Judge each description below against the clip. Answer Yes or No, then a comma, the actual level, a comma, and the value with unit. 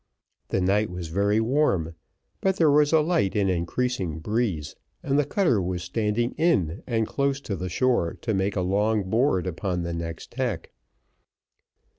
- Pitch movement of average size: No, wide, 6.1 semitones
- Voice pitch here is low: Yes, low, 105 Hz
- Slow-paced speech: No, average, 160 wpm